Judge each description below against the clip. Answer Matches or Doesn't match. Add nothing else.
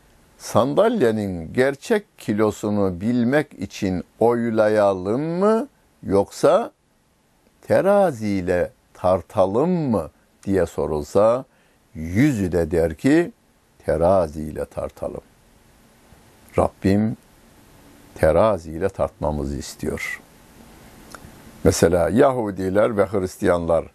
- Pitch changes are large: Doesn't match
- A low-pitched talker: Matches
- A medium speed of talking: Doesn't match